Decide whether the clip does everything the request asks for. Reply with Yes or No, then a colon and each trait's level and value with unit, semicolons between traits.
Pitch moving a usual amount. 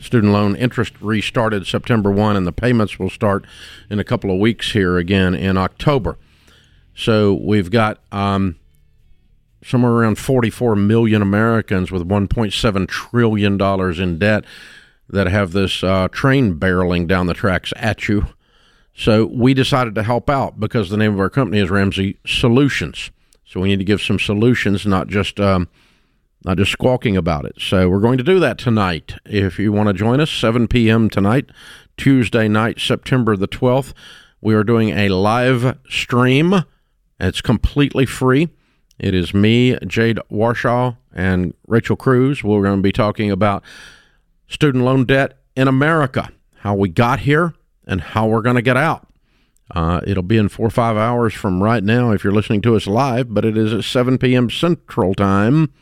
Yes: average, 4.0 semitones